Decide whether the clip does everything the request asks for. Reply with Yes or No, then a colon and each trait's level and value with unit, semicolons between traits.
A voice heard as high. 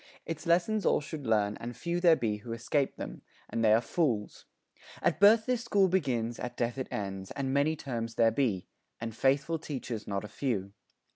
No: low, 125 Hz